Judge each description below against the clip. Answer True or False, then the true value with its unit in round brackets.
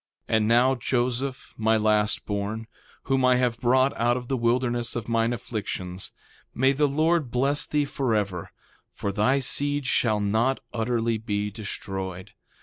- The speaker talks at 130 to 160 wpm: True (150 wpm)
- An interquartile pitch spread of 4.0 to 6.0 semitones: False (3.5 semitones)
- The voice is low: True (120 Hz)